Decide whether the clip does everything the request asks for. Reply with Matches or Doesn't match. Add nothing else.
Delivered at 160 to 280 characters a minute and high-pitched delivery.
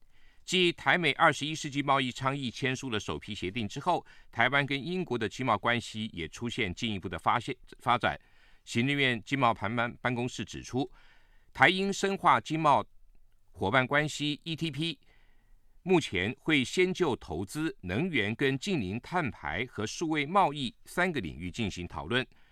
Doesn't match